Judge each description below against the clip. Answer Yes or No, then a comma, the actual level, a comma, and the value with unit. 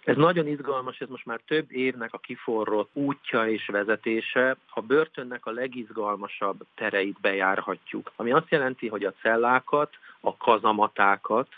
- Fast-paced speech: No, average, 140 wpm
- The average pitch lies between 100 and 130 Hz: Yes, low, 120 Hz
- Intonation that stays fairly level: No, average, 3.3 semitones